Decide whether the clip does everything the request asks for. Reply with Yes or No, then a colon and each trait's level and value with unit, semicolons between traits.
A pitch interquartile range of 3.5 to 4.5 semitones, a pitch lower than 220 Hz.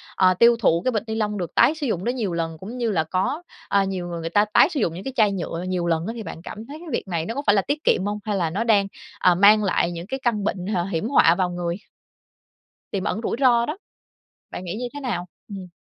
No: average, 4.9 semitones; high, 200 Hz